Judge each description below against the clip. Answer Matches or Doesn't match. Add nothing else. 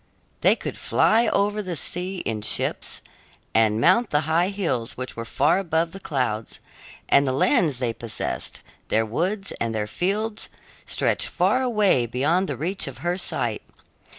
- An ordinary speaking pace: Matches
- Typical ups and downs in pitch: Doesn't match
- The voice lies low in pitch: Doesn't match